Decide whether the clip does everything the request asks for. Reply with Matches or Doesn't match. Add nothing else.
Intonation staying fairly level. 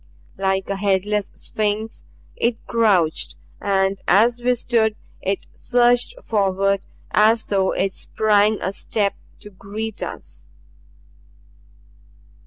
Matches